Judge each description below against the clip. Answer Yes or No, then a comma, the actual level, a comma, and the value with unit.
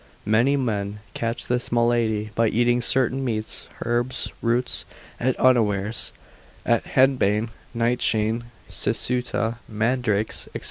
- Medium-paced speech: No, slow, 105 wpm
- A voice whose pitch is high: No, low, 115 Hz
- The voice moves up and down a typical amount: No, narrow, 2.2 semitones